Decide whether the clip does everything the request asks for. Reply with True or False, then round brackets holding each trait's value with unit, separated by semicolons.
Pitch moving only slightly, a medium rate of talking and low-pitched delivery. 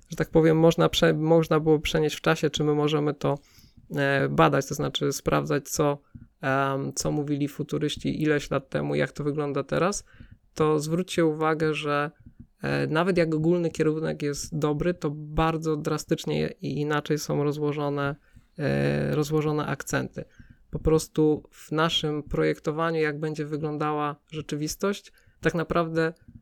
False (1.8 semitones; 130 wpm; 150 Hz)